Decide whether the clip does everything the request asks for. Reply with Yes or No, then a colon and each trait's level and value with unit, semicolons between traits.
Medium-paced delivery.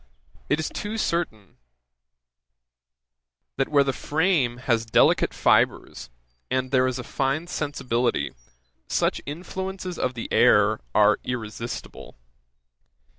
No: slow, 110 wpm